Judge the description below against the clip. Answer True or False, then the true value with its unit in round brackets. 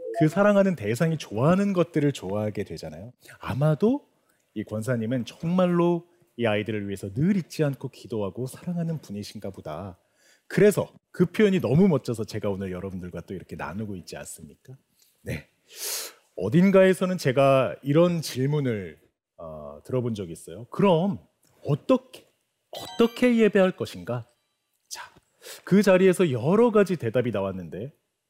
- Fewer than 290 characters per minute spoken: False (315 characters per minute)